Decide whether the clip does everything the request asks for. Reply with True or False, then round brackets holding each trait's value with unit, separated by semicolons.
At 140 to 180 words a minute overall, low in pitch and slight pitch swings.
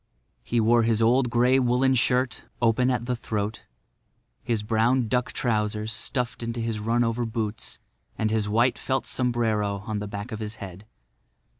True (165 wpm; 115 Hz; 2.3 semitones)